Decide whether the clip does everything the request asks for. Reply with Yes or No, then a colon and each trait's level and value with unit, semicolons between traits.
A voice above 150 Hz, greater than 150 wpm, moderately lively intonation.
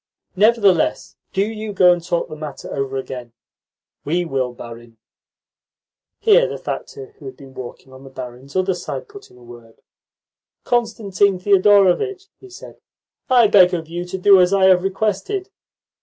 No: medium, 185 Hz; average, 165 wpm; wide, 7.9 semitones